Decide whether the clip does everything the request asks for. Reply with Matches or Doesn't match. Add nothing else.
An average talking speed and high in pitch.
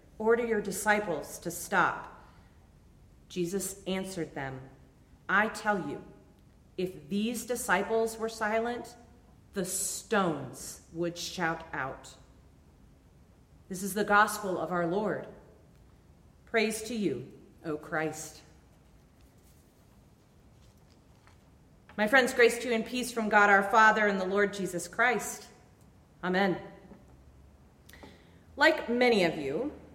Doesn't match